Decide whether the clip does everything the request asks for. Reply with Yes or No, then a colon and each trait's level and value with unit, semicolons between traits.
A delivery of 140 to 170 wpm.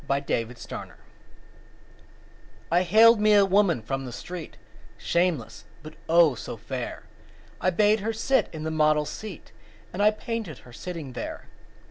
Yes: average, 145 wpm